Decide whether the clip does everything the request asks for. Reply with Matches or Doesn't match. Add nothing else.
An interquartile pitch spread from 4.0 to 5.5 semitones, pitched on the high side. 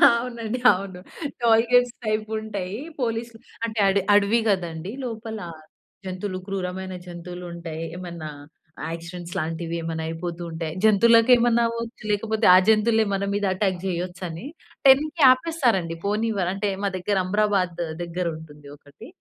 Matches